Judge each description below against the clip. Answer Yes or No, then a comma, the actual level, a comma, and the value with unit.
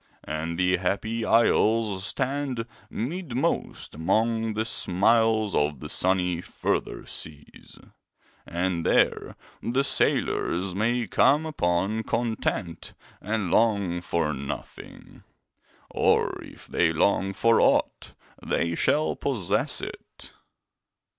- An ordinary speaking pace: No, slow, 100 wpm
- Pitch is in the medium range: No, low, 100 Hz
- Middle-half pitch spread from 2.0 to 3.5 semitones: No, average, 4.8 semitones